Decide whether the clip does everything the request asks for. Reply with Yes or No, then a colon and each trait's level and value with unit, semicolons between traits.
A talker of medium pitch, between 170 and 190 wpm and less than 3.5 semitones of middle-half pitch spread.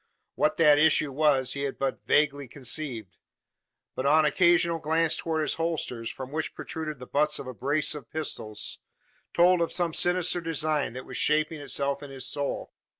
Yes: medium, 150 Hz; average, 175 wpm; average, 2.8 semitones